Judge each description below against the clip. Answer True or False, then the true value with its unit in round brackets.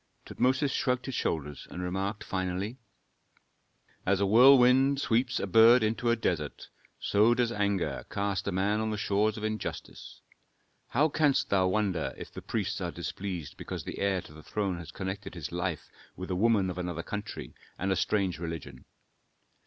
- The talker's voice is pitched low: True (100 Hz)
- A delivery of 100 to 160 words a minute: False (170 wpm)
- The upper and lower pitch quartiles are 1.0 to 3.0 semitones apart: False (4.1 semitones)